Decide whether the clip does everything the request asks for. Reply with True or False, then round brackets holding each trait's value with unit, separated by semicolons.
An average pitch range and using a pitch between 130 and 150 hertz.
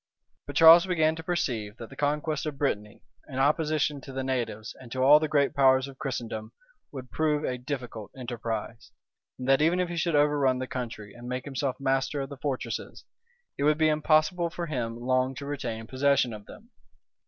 True (3.2 semitones; 135 Hz)